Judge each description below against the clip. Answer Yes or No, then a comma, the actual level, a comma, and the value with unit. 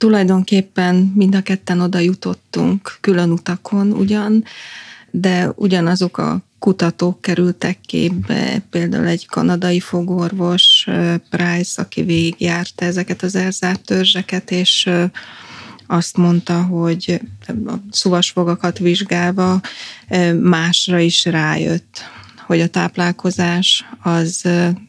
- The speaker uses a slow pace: Yes, slow, 95 wpm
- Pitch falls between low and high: Yes, medium, 180 Hz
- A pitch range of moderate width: No, narrow, 1.5 semitones